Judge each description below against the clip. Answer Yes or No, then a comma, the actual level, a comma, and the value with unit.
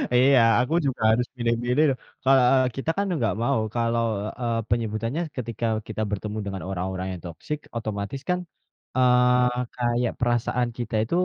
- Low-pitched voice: Yes, low, 120 Hz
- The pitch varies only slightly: Yes, narrow, 2.2 semitones